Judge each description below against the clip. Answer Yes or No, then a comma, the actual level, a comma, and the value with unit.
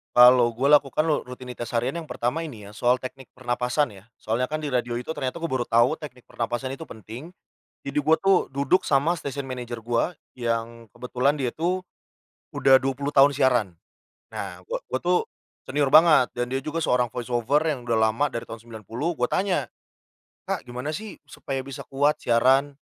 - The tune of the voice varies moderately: Yes, average, 3.7 semitones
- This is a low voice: Yes, low, 130 Hz